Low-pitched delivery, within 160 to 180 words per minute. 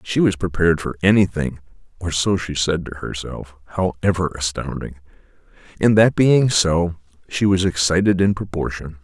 No: very low, 85 Hz; average, 145 wpm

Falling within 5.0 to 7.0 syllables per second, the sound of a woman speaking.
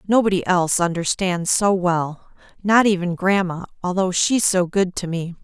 No: 4.7 syllables/s; female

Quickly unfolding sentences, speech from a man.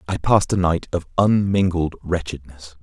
No: average, 150 wpm; male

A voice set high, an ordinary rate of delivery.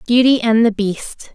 Yes: high, 230 Hz; average, 180 wpm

